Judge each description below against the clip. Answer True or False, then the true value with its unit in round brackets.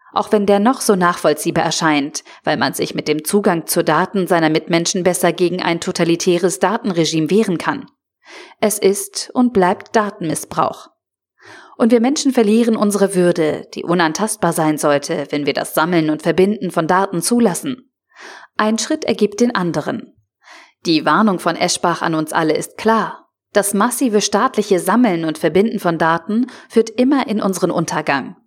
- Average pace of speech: True (160 wpm)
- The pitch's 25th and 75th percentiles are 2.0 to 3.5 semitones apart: False (4.7 semitones)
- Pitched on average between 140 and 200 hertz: True (185 Hz)